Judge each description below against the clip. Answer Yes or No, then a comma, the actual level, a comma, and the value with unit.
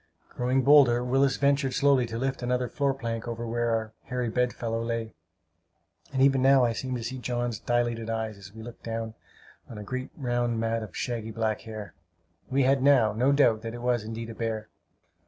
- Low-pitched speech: Yes, low, 120 Hz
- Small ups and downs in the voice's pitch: Yes, narrow, 2.3 semitones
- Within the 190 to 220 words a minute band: Yes, average, 200 wpm